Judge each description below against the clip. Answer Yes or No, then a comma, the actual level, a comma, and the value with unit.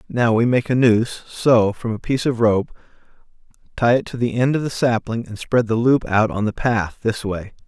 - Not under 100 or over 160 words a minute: No, fast, 205 wpm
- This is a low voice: Yes, low, 115 Hz